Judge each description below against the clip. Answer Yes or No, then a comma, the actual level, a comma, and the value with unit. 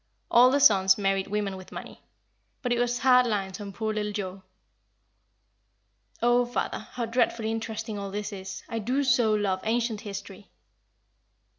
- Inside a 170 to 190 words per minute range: No, average, 155 wpm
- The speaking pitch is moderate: No, high, 215 Hz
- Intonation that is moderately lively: Yes, average, 3.3 semitones